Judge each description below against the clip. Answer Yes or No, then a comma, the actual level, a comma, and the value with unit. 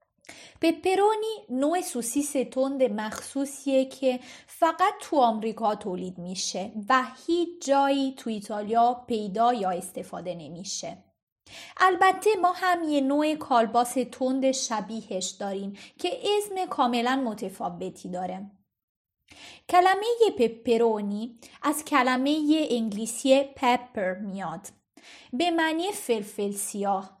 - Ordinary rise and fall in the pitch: No, wide, 6.3 semitones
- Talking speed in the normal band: No, slow, 100 wpm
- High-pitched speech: Yes, very high, 250 Hz